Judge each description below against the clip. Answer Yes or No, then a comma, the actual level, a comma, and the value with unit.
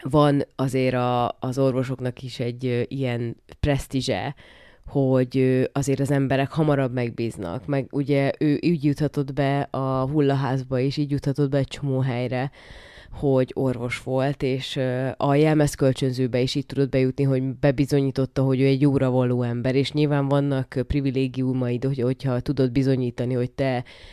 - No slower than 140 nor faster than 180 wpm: Yes, average, 145 wpm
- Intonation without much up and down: Yes, narrow, 1.7 semitones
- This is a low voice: Yes, low, 130 Hz